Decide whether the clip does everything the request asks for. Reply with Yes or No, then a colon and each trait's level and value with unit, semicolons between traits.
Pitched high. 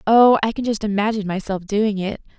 Yes: high, 210 Hz